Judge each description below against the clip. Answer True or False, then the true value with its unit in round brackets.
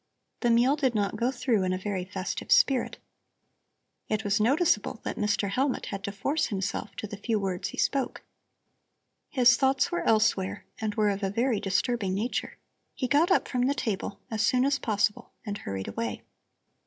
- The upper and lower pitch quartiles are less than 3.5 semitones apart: False (4.2 semitones)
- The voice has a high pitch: True (215 Hz)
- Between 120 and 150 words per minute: False (180 wpm)